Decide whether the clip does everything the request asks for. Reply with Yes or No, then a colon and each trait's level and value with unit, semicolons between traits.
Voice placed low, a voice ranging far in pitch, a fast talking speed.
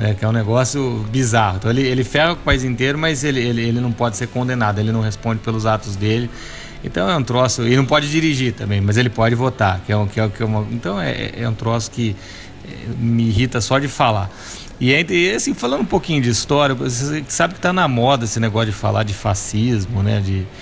No: low, 115 Hz; average, 3.3 semitones; fast, 235 wpm